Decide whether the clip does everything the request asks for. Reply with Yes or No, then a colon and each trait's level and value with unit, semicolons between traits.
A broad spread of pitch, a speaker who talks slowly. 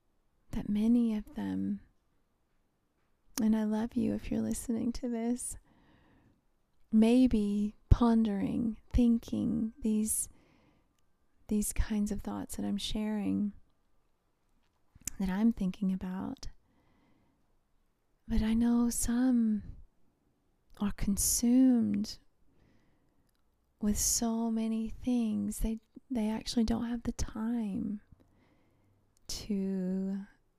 No: narrow, 2.5 semitones; slow, 90 wpm